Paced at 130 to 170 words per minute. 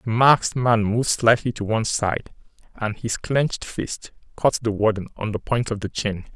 No: average, 200 wpm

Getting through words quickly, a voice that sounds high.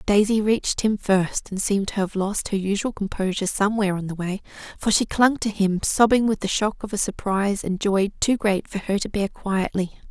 Yes: fast, 225 wpm; high, 200 Hz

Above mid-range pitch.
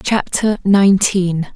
Yes: high, 195 Hz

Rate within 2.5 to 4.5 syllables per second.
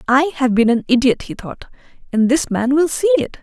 No: 5.3 syllables/s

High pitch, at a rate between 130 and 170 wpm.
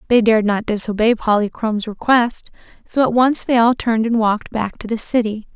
No: high, 225 Hz; average, 195 wpm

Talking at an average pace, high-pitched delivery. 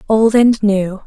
Yes: average, 170 wpm; high, 210 Hz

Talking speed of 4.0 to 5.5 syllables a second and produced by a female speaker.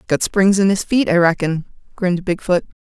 Yes: 5.4 syllables/s; female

